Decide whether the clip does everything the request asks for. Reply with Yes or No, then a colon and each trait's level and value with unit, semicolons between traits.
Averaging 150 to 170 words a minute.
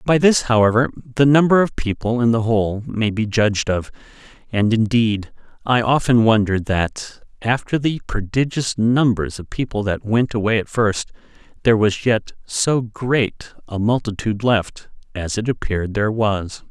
Yes: average, 160 wpm